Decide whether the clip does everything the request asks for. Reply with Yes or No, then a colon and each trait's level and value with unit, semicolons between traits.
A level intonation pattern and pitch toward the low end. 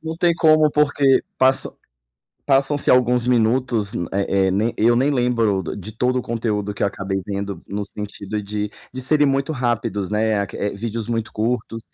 No: average, 4.1 semitones; low, 115 Hz